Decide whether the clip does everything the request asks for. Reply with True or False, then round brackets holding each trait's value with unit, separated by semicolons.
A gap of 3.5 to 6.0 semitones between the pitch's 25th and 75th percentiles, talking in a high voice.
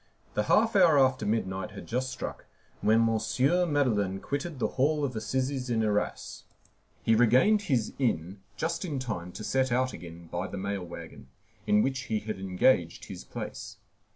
False (4.8 semitones; 120 Hz)